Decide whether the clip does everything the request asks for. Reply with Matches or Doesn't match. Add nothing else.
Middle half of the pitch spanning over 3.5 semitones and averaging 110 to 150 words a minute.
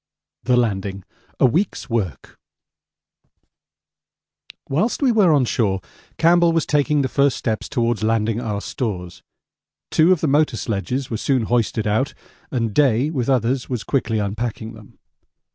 Matches